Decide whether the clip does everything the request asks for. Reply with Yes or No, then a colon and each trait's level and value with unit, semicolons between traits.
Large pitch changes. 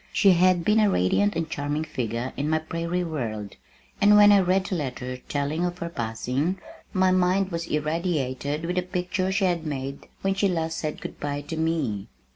No: average, 4.3 semitones